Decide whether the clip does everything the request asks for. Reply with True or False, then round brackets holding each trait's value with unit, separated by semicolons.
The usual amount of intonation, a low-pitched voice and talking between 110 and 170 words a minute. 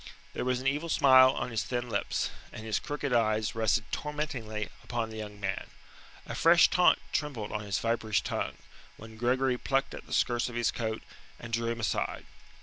False (3.0 semitones; 120 Hz; 190 wpm)